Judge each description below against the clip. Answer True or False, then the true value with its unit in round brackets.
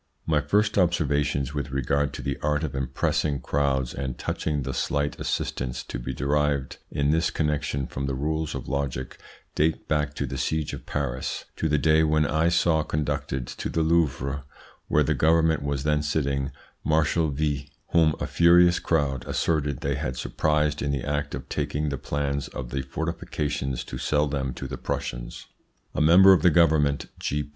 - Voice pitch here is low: True (75 Hz)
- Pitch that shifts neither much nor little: False (2.2 semitones)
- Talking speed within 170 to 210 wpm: True (180 wpm)